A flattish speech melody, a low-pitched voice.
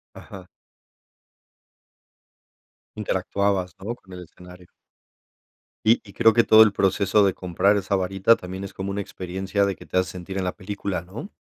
Yes: narrow, 1.7 semitones; very low, 95 Hz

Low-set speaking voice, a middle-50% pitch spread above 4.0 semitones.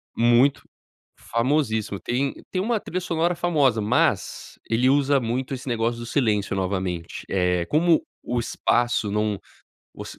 Yes: low, 120 Hz; average, 5.0 semitones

